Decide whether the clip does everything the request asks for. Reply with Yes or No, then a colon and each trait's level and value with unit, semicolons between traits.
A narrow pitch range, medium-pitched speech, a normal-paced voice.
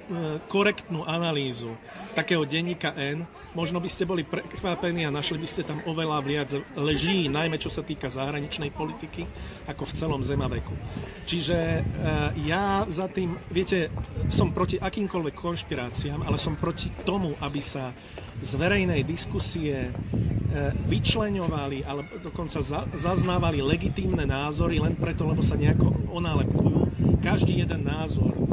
No: average, 3.7 semitones; medium, 160 Hz; average, 130 wpm